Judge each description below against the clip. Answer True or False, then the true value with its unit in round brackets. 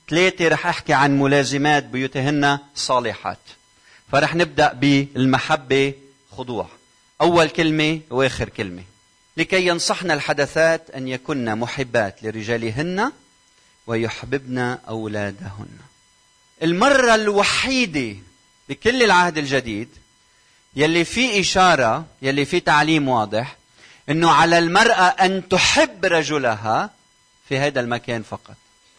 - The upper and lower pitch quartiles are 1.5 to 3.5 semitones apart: False (5.8 semitones)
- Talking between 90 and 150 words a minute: True (95 wpm)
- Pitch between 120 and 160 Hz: True (140 Hz)